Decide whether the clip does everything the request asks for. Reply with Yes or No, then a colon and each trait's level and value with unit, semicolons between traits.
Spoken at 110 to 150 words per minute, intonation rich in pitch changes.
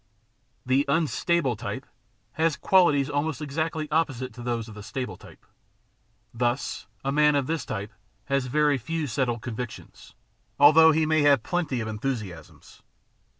No: average, 145 wpm; average, 4.4 semitones